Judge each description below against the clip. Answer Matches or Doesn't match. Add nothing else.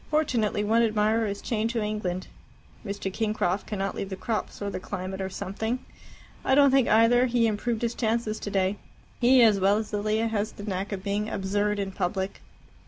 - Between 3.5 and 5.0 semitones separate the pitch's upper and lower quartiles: Doesn't match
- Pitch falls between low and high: Doesn't match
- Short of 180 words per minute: Doesn't match